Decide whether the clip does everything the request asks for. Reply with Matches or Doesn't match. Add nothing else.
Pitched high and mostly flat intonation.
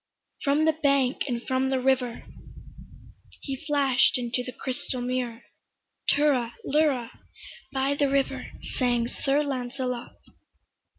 Matches